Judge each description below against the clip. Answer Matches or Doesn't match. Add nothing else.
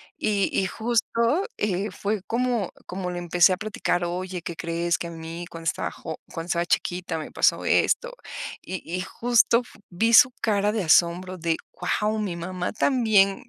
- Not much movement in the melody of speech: Doesn't match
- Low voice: Doesn't match